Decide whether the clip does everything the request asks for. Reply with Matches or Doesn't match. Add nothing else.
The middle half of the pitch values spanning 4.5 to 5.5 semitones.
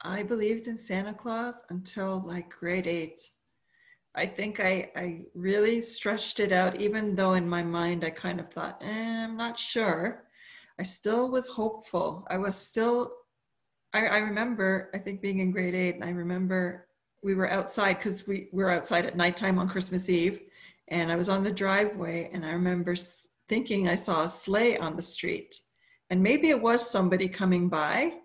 Doesn't match